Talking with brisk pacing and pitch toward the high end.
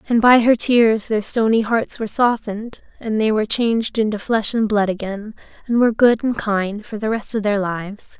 Yes: fast, 210 wpm; high, 220 Hz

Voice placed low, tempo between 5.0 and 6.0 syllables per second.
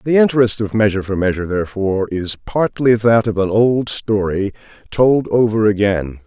Yes: low, 105 Hz; 5.2 syllables/s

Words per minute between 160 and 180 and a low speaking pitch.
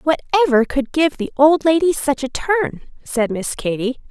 No: average, 175 wpm; very high, 285 Hz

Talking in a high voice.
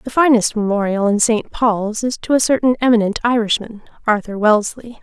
Yes: high, 225 Hz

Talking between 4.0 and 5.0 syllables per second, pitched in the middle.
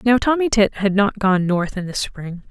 No: 4.6 syllables/s; high, 205 Hz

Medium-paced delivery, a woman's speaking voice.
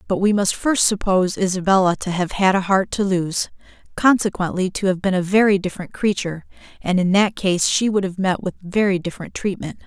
Yes: average, 195 wpm; female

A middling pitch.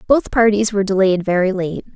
No: high, 200 Hz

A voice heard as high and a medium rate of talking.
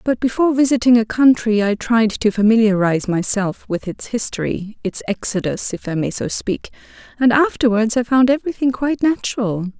Yes: high, 230 Hz; average, 165 wpm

